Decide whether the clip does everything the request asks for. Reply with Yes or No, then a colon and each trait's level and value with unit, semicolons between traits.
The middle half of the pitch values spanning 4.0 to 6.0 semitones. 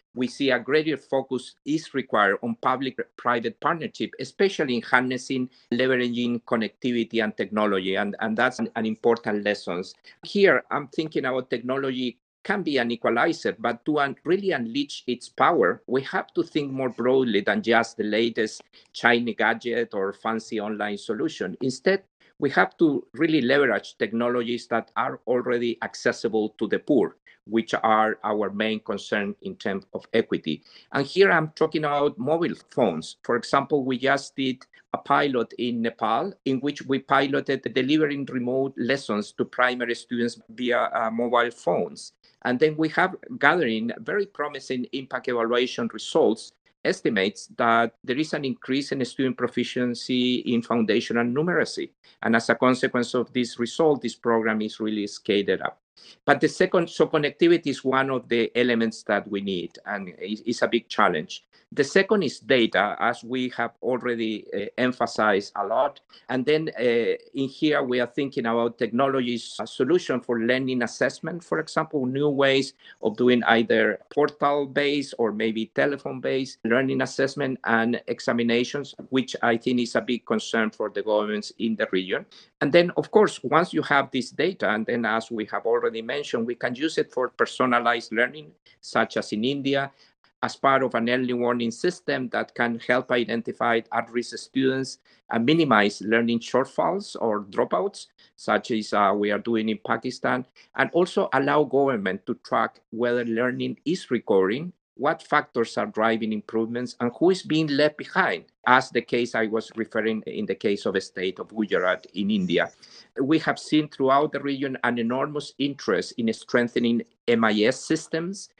No: average, 3.2 semitones